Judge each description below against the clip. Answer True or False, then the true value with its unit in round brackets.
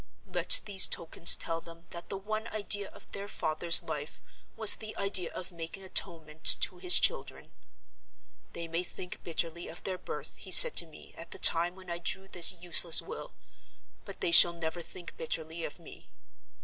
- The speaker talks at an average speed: True (180 wpm)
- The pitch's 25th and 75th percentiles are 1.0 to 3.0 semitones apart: True (2.6 semitones)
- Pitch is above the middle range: False (175 Hz)